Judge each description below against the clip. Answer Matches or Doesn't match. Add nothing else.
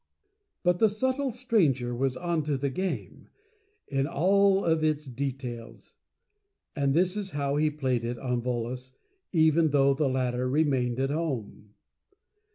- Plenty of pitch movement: Doesn't match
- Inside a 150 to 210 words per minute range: Doesn't match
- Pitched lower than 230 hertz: Matches